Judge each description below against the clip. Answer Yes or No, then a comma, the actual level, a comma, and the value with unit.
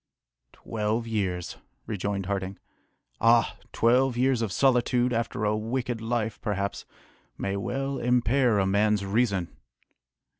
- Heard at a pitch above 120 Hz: No, low, 110 Hz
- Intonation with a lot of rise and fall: No, average, 3.4 semitones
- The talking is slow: Yes, slow, 115 wpm